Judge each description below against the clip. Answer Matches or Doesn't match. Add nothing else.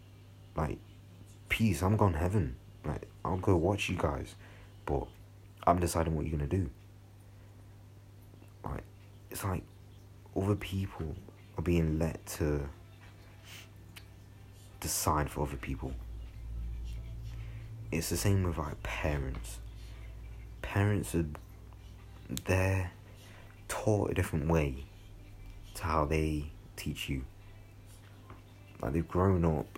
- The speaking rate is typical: Doesn't match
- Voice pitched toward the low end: Matches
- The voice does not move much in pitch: Doesn't match